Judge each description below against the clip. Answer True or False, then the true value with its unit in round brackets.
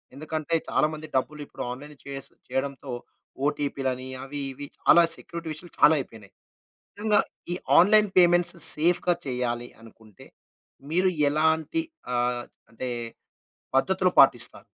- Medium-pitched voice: True (150 Hz)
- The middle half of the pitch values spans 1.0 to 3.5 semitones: False (4.7 semitones)